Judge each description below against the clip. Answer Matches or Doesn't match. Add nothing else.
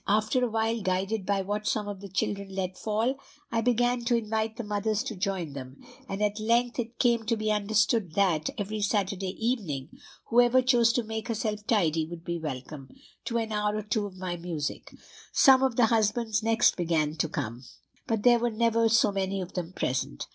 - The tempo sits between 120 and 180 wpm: Doesn't match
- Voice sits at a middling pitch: Doesn't match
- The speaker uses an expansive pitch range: Doesn't match